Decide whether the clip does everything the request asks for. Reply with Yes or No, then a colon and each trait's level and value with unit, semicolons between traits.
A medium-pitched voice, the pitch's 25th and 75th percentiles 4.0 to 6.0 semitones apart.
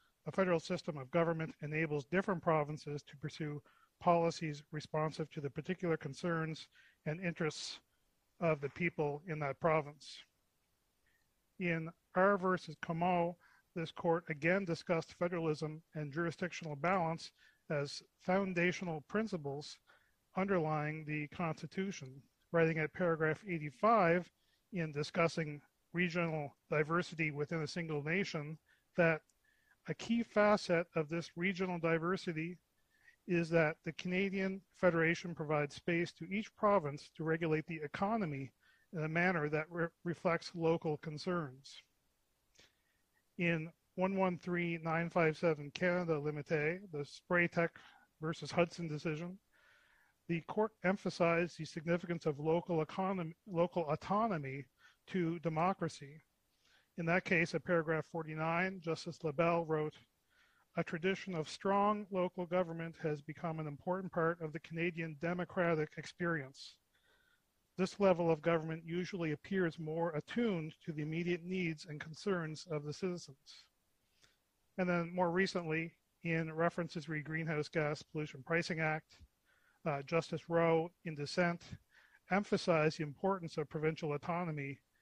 No: medium, 165 Hz; narrow, 2.4 semitones